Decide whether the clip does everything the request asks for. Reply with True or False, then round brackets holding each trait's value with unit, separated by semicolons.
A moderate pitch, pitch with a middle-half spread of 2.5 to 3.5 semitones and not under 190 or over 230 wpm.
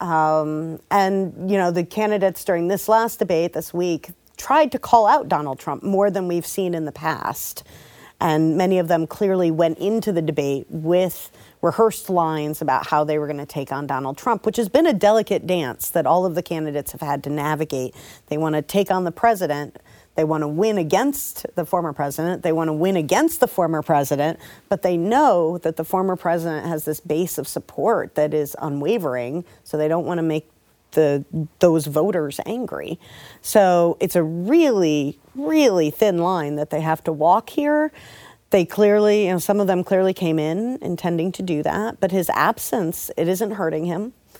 False (170 Hz; 4.0 semitones; 195 wpm)